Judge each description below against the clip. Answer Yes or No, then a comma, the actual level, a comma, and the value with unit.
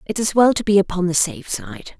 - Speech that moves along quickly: Yes, fast, 270 wpm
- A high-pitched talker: Yes, high, 195 Hz